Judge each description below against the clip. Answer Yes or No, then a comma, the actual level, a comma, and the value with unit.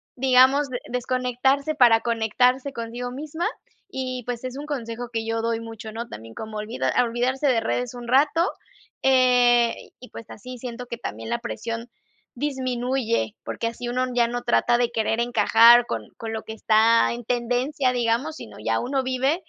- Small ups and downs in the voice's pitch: Yes, narrow, 2.0 semitones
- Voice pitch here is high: Yes, high, 245 Hz